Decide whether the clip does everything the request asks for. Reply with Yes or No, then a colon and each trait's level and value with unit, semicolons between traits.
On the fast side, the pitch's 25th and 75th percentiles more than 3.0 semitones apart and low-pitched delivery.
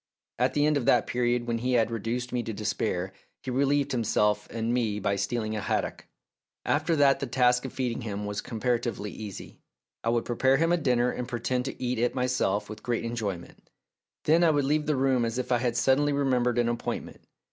No: fast, 210 wpm; average, 2.7 semitones; low, 120 Hz